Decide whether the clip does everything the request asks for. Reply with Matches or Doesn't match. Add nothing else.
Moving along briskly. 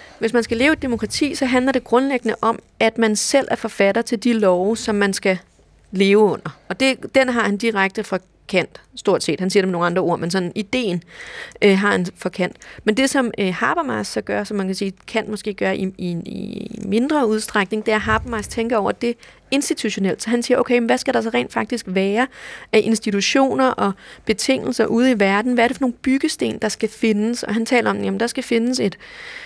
Matches